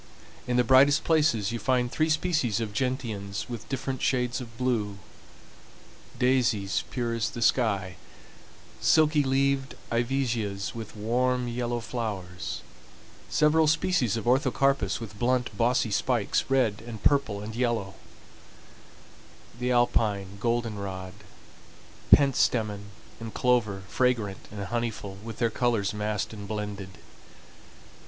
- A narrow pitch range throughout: No, average, 3.6 semitones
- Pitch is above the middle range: No, low, 120 Hz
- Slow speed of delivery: Yes, slow, 120 wpm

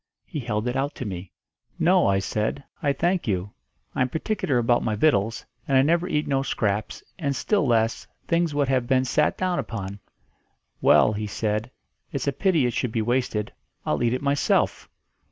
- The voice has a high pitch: No, low, 125 Hz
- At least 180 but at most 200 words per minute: Yes, average, 190 wpm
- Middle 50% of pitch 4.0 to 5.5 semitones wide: Yes, average, 4.9 semitones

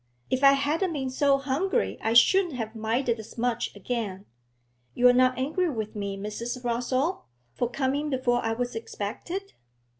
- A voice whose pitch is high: Yes, very high, 250 Hz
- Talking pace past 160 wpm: No, average, 155 wpm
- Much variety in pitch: No, average, 3.5 semitones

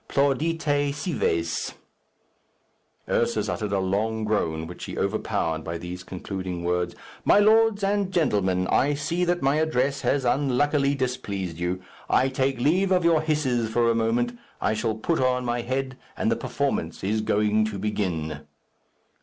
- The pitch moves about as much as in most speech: No, wide, 6.8 semitones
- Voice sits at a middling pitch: No, low, 120 Hz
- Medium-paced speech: Yes, average, 155 wpm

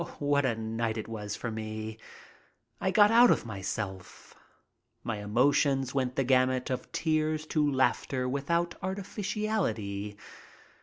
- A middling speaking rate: No, slow, 130 wpm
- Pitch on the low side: Yes, low, 130 Hz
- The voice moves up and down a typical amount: No, wide, 5.9 semitones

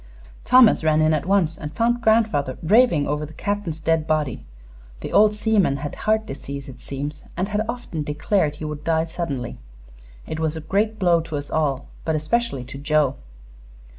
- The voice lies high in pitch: No, medium, 160 Hz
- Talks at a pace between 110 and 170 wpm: No, average, 180 wpm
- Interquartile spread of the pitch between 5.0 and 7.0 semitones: Yes, wide, 5.6 semitones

